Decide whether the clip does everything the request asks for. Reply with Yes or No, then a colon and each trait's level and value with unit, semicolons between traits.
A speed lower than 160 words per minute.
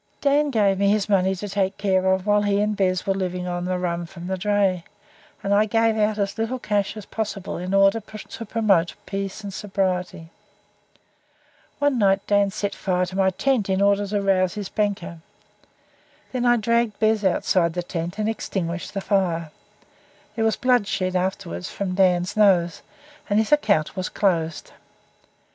No: average, 170 wpm